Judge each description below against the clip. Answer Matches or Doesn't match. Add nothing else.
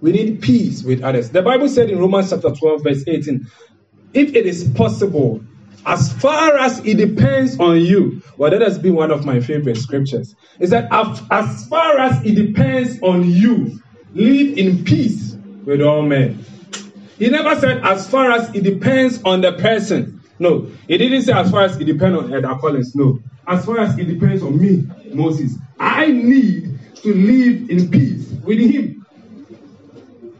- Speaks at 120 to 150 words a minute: Doesn't match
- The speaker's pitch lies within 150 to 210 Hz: Matches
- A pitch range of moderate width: Doesn't match